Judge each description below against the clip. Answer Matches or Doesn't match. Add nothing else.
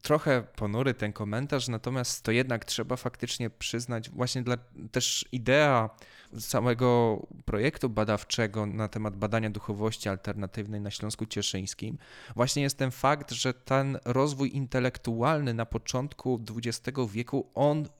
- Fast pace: Doesn't match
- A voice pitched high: Doesn't match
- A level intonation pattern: Doesn't match